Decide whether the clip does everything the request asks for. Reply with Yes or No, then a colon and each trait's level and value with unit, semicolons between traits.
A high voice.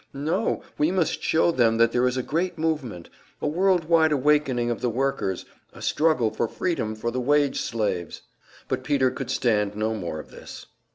No: low, 130 Hz